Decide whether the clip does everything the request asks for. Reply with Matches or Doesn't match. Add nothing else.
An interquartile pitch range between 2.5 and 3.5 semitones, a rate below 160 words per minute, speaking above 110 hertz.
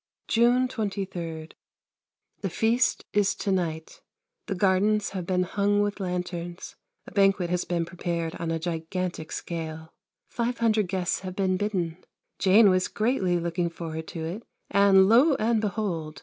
Matches